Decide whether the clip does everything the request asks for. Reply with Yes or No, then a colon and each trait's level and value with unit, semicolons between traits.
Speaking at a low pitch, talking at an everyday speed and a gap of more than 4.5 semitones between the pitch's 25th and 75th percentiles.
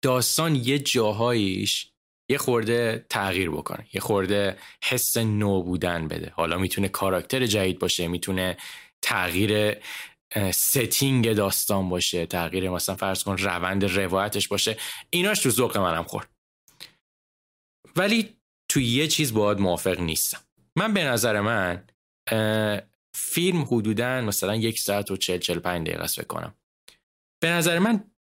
Yes: low, 105 Hz; average, 125 wpm; average, 5.1 semitones